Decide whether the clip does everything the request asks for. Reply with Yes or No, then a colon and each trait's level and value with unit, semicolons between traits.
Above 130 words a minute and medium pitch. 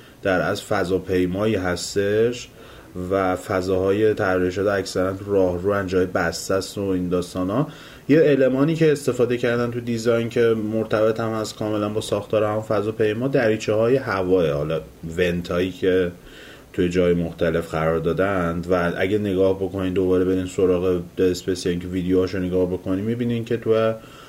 No: fast, 155 wpm; very low, 95 Hz